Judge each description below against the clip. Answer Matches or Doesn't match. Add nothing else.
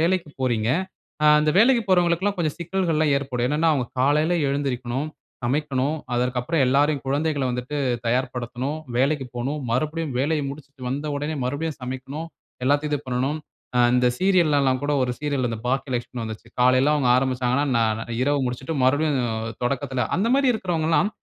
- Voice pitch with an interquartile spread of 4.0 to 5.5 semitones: Doesn't match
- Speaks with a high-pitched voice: Doesn't match